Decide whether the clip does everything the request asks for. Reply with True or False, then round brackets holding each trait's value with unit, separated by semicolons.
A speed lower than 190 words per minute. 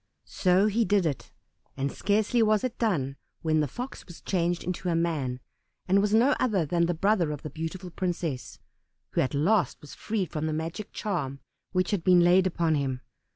False (195 wpm)